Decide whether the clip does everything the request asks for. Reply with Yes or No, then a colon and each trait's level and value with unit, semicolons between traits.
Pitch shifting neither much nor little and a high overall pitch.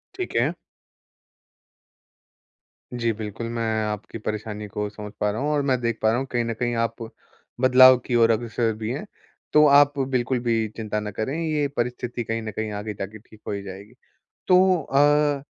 No: average, 3.2 semitones; low, 115 Hz